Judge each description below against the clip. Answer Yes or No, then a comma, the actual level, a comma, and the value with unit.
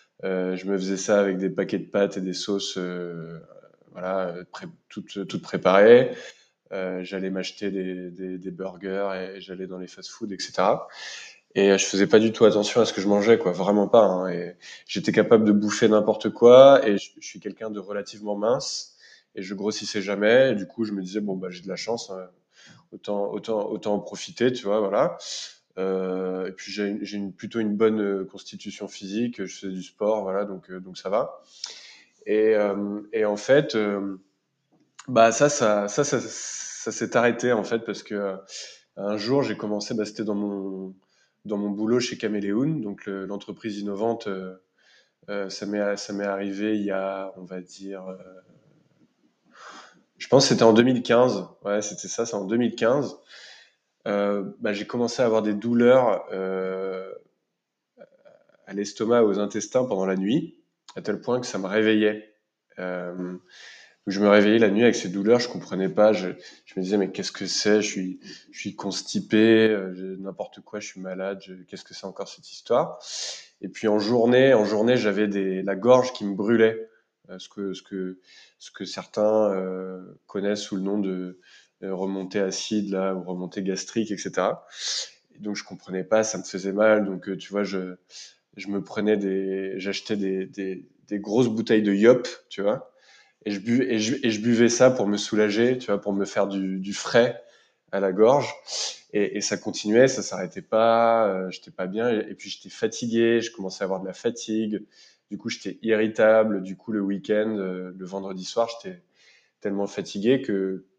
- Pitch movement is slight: Yes, narrow, 2.3 semitones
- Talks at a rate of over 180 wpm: Yes, average, 190 wpm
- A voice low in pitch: Yes, low, 100 Hz